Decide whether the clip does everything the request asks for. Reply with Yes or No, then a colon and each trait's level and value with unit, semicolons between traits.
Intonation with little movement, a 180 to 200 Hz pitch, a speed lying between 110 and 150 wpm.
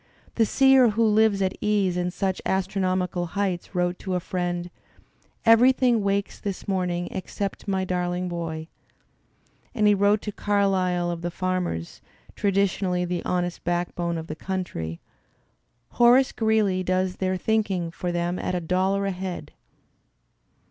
Yes: narrow, 2.3 semitones; medium, 185 Hz; average, 140 wpm